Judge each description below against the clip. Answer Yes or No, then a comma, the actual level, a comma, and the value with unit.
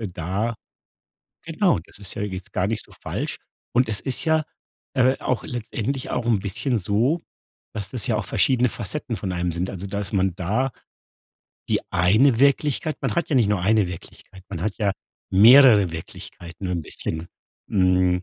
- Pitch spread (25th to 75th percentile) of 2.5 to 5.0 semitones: No, wide, 5.4 semitones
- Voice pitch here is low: Yes, low, 105 Hz